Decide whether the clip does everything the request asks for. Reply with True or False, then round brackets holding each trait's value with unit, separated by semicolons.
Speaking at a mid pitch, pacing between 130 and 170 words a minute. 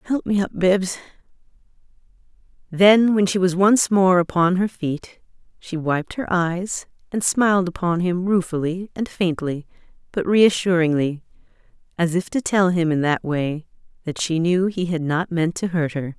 True (180 Hz; 165 wpm)